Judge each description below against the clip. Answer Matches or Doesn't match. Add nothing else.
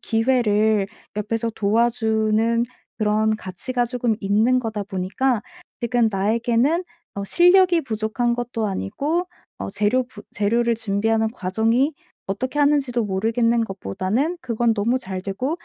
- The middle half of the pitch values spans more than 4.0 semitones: Doesn't match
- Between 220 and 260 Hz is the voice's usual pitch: Matches